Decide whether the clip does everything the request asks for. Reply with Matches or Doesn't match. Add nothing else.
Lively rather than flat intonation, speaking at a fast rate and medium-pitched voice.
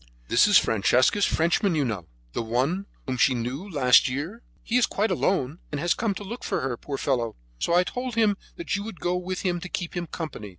Matches